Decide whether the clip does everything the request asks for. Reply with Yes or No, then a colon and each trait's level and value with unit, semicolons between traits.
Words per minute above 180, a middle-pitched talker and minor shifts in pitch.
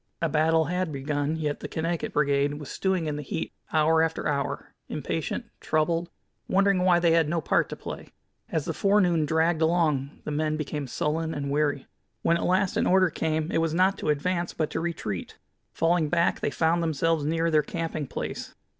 Yes: average, 190 wpm; medium, 160 Hz; narrow, 2.1 semitones